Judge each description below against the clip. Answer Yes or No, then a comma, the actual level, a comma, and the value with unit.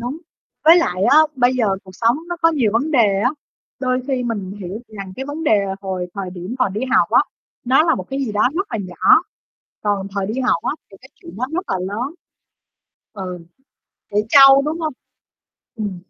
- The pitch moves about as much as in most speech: No, wide, 5.8 semitones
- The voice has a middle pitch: No, high, 230 Hz